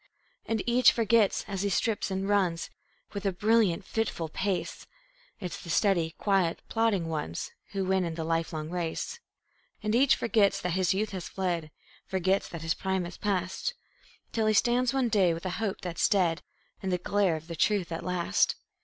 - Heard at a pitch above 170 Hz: Yes, high, 190 Hz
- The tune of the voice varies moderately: Yes, average, 3.6 semitones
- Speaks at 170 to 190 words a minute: Yes, average, 180 wpm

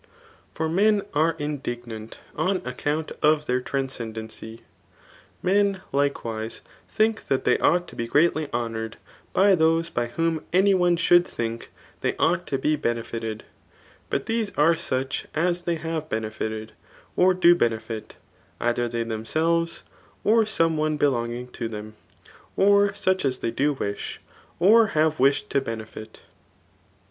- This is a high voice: No, medium, 150 Hz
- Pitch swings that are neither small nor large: No, wide, 6.8 semitones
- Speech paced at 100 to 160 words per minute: Yes, average, 145 wpm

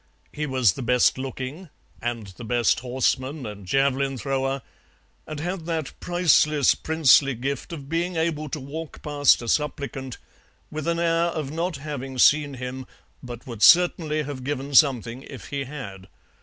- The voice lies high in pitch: No, medium, 140 Hz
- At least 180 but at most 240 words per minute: No, average, 155 wpm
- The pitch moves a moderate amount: Yes, average, 3.3 semitones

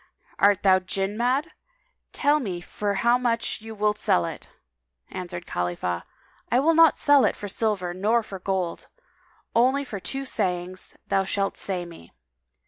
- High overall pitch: Yes, high, 200 Hz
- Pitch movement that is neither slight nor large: Yes, average, 4.5 semitones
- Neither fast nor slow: Yes, average, 160 wpm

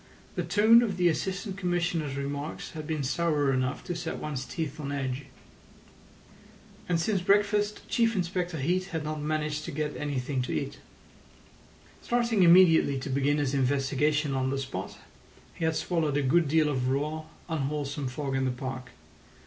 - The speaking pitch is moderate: Yes, medium, 150 Hz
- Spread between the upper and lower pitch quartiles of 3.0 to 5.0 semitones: Yes, average, 4.2 semitones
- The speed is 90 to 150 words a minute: No, average, 165 wpm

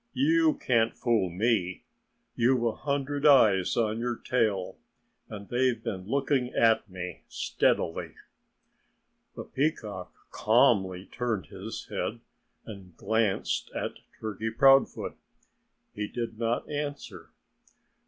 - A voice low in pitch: Yes, low, 115 Hz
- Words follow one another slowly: Yes, slow, 110 wpm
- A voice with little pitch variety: No, average, 4.3 semitones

